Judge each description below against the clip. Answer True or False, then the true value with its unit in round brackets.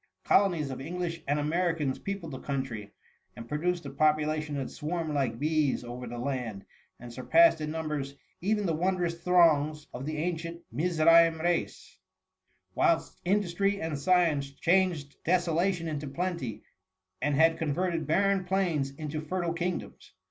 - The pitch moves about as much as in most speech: True (3.7 semitones)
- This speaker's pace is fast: False (150 wpm)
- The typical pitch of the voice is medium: True (160 Hz)